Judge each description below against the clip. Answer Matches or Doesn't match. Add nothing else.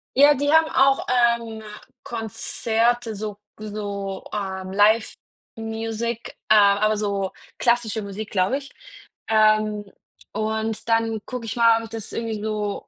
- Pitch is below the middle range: Doesn't match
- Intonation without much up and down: Matches